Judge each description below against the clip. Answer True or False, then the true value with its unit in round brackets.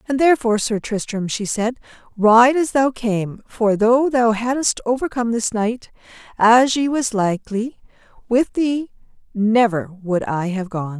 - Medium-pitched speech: False (225 Hz)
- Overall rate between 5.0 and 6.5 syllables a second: False (4.4 syllables/s)